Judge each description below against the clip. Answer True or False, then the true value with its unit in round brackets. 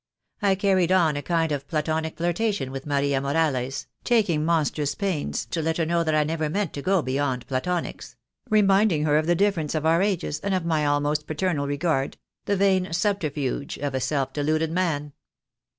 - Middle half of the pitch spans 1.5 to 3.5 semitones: False (4.0 semitones)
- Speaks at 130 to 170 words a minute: False (190 wpm)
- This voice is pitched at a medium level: True (160 Hz)